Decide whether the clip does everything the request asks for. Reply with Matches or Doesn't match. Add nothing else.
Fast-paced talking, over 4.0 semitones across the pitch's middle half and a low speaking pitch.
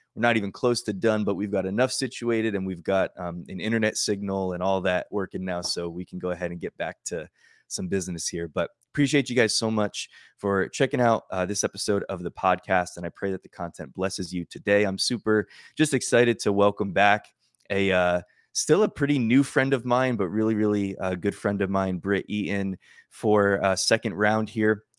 Doesn't match